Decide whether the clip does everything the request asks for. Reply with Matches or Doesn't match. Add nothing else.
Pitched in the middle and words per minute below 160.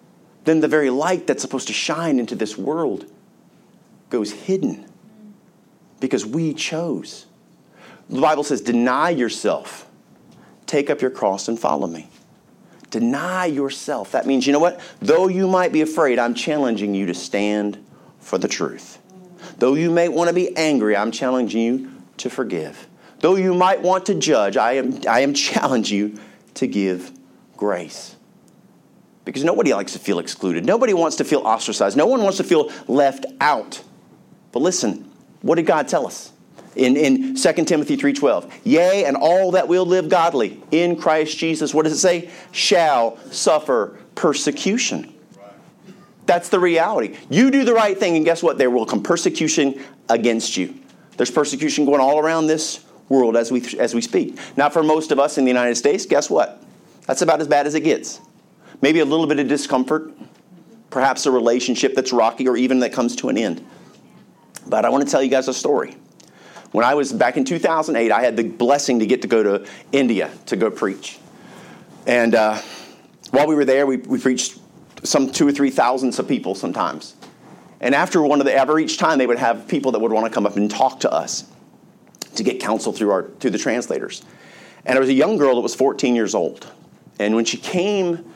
Doesn't match